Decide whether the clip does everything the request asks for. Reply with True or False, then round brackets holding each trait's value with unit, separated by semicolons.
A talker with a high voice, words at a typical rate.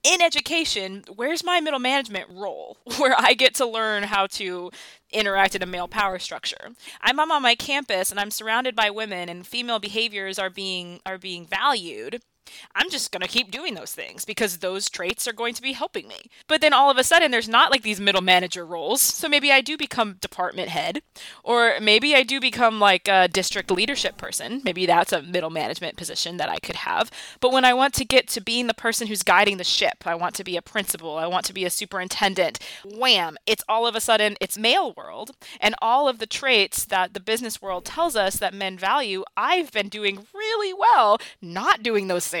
False (215 Hz; 215 wpm)